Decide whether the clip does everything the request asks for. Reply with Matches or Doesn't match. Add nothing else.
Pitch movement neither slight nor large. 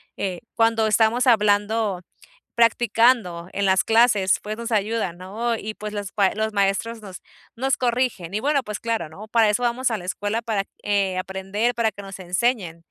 Matches